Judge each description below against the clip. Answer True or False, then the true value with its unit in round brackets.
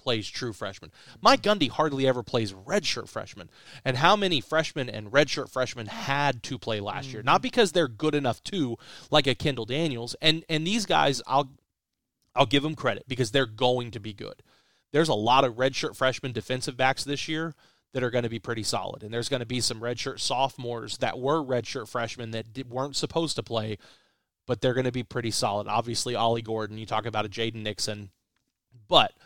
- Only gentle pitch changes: False (3.5 semitones)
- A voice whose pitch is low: True (125 Hz)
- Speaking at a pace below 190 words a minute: False (205 wpm)